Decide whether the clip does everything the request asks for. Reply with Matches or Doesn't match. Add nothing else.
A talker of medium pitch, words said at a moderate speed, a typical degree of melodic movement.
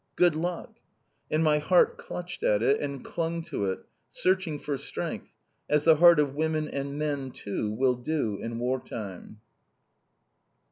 Matches